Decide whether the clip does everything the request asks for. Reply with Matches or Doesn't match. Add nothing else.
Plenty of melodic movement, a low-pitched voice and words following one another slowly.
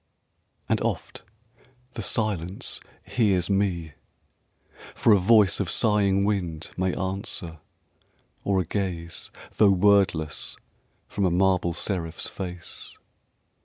Doesn't match